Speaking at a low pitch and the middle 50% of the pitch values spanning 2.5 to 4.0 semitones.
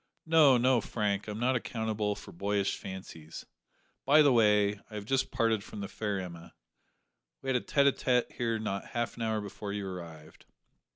Yes: low, 105 Hz; average, 3.6 semitones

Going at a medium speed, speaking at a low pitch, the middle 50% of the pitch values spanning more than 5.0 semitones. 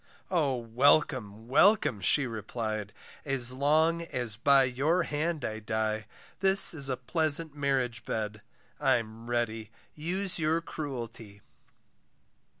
No: slow, 115 wpm; low, 130 Hz; wide, 5.6 semitones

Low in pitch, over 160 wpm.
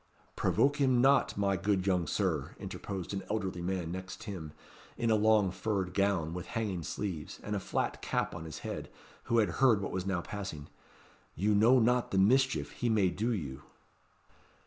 Yes: low, 100 Hz; average, 180 wpm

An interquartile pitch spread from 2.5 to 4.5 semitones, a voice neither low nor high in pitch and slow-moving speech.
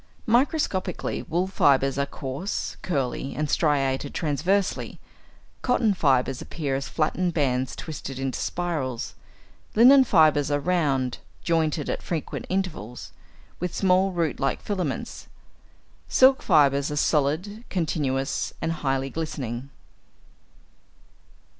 No: average, 5.0 semitones; medium, 155 Hz; slow, 110 wpm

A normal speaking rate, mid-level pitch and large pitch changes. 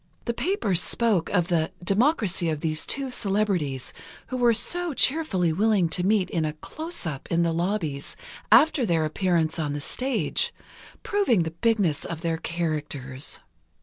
Yes: average, 150 wpm; medium, 180 Hz; wide, 6.3 semitones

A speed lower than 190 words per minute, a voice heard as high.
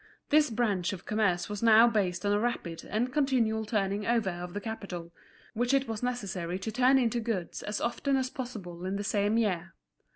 No: average, 195 wpm; high, 215 Hz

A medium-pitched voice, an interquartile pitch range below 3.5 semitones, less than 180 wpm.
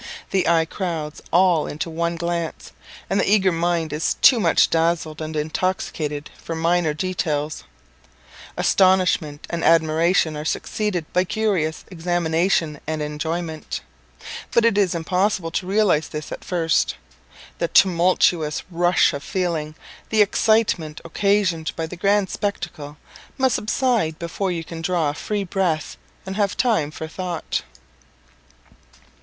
Yes: medium, 170 Hz; average, 3.1 semitones; slow, 135 wpm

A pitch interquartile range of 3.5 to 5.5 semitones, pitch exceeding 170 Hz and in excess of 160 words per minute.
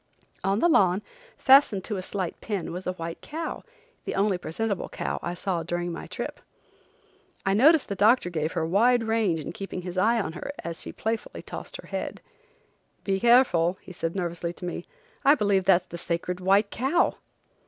Yes: average, 4.3 semitones; high, 190 Hz; average, 185 wpm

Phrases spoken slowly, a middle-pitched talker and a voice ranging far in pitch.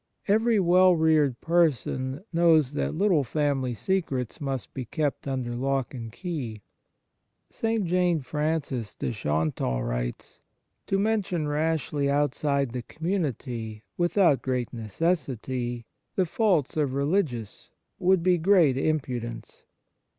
Yes: slow, 120 wpm; medium, 145 Hz; wide, 5.8 semitones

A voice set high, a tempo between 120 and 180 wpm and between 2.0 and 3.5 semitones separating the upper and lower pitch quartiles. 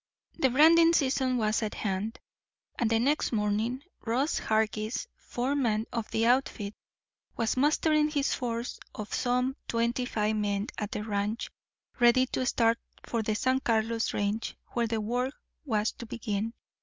Yes: high, 230 Hz; average, 150 wpm; average, 3.0 semitones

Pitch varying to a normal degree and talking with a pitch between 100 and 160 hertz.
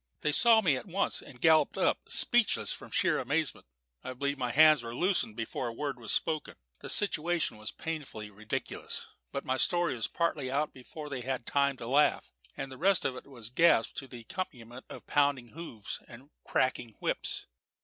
Yes: average, 4.5 semitones; low, 135 Hz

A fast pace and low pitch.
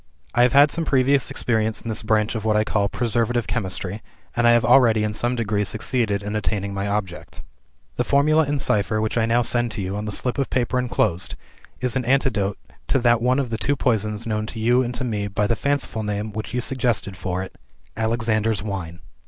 Yes: fast, 220 wpm; low, 110 Hz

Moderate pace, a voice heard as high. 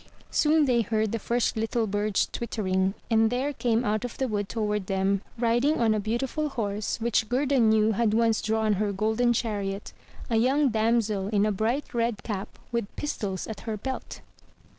Yes: average, 185 wpm; high, 220 Hz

